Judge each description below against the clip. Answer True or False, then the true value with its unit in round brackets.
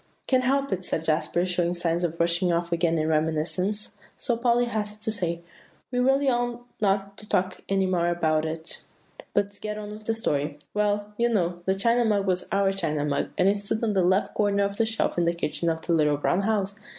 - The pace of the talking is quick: True (220 wpm)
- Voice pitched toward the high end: True (195 Hz)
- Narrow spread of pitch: False (3.9 semitones)